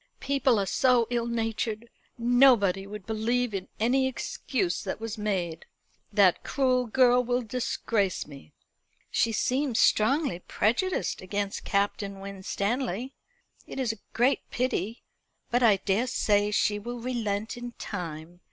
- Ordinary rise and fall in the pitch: Yes, average, 3.7 semitones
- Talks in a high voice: Yes, high, 225 Hz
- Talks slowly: Yes, slow, 130 wpm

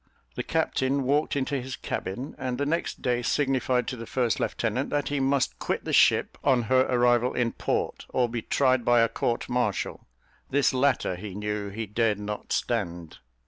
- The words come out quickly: No, average, 185 wpm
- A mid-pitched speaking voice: No, low, 125 Hz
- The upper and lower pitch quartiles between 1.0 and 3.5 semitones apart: Yes, average, 2.9 semitones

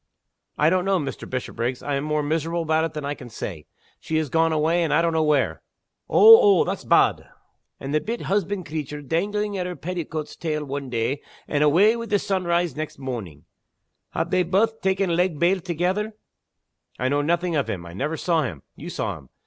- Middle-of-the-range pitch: Yes, medium, 160 Hz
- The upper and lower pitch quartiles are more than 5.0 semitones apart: No, average, 4.1 semitones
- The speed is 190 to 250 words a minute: Yes, fast, 205 wpm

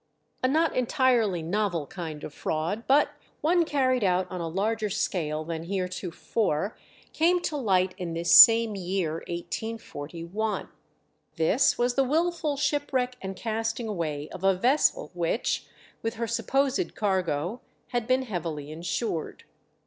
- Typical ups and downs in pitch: No, wide, 6.6 semitones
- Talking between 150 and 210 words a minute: No, slow, 135 wpm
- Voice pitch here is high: Yes, high, 205 Hz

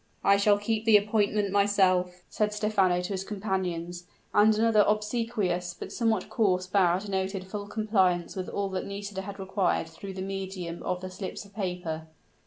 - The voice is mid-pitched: No, high, 195 Hz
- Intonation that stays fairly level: Yes, narrow, 2.3 semitones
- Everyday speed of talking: Yes, average, 170 wpm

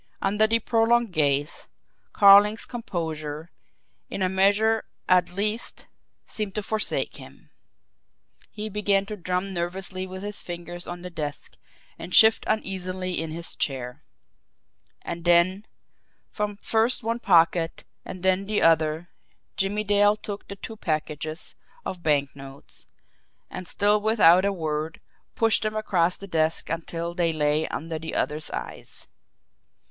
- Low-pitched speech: No, medium, 185 Hz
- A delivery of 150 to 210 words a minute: No, slow, 135 wpm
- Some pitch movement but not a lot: Yes, average, 4.2 semitones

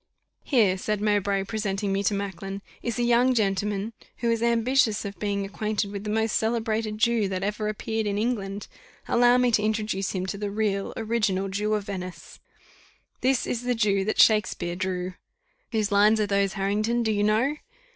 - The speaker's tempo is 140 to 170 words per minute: No, average, 180 wpm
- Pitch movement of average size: No, narrow, 2.2 semitones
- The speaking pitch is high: Yes, high, 210 Hz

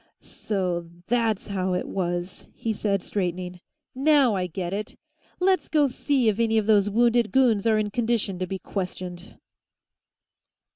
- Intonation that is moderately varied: Yes, average, 4.1 semitones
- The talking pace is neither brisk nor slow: Yes, average, 150 wpm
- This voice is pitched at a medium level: No, high, 205 Hz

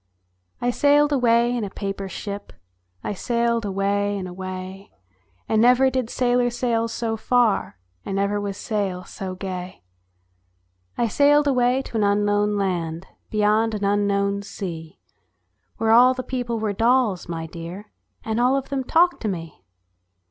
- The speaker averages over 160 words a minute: No, average, 150 wpm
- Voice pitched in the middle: No, high, 210 Hz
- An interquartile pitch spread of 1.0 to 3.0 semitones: No, average, 3.7 semitones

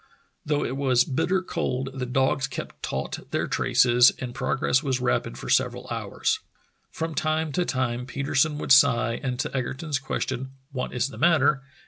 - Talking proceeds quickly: No, average, 165 wpm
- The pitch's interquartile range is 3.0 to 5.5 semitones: No, narrow, 2.4 semitones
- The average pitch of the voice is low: Yes, low, 130 Hz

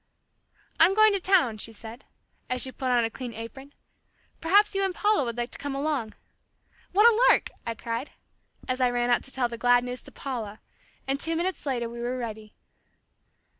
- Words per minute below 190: No, average, 200 wpm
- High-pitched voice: Yes, very high, 255 Hz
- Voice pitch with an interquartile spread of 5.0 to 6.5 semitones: Yes, wide, 5.6 semitones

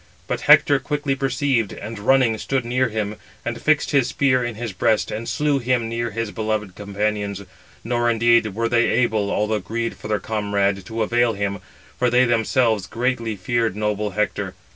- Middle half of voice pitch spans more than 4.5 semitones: No, narrow, 2.5 semitones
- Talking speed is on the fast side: No, average, 175 wpm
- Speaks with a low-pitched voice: Yes, low, 115 Hz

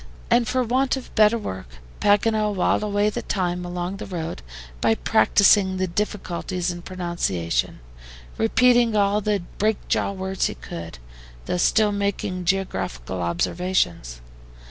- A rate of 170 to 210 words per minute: No, slow, 135 wpm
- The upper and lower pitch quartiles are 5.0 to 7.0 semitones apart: No, average, 3.4 semitones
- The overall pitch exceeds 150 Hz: Yes, high, 190 Hz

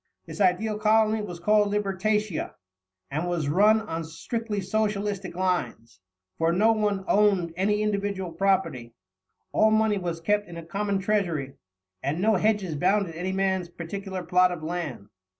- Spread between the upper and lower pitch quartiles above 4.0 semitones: No, average, 3.4 semitones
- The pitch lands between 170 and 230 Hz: Yes, high, 190 Hz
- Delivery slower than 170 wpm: Yes, average, 150 wpm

